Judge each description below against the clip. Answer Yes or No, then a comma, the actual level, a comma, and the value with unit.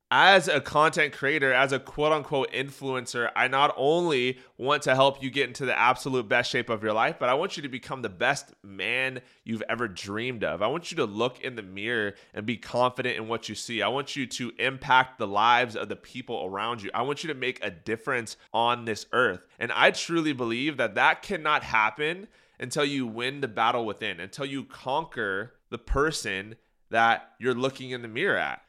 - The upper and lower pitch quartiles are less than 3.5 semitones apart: Yes, average, 2.9 semitones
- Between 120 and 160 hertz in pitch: Yes, low, 125 Hz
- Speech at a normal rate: No, fast, 210 wpm